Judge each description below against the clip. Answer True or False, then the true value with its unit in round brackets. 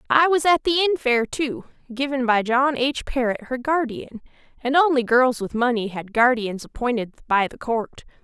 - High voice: True (255 Hz)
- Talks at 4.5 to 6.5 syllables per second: True (5.2 syllables/s)